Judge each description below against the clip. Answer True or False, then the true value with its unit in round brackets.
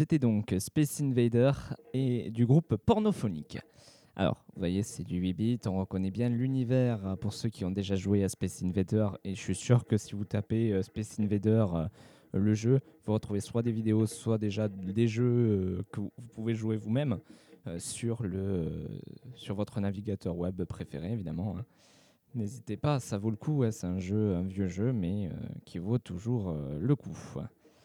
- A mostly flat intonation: False (3.9 semitones)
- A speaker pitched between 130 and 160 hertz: False (110 Hz)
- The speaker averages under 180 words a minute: True (170 wpm)